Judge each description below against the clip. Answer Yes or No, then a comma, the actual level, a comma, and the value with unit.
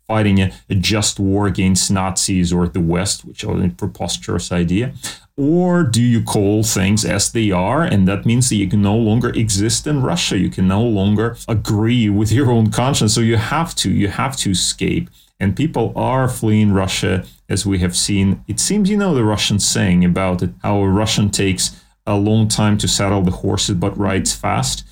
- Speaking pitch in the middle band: No, low, 105 Hz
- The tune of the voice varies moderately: Yes, average, 3.0 semitones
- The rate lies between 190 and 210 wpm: Yes, average, 200 wpm